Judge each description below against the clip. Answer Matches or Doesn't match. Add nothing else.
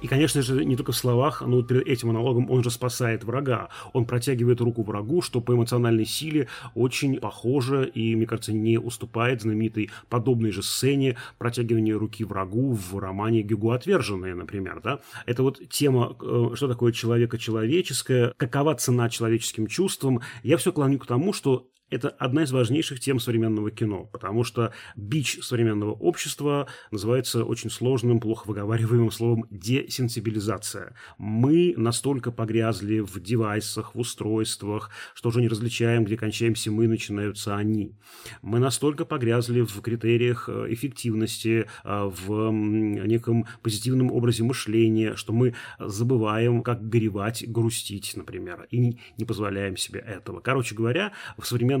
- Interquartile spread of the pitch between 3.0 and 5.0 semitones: Doesn't match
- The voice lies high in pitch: Doesn't match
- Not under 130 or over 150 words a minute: Matches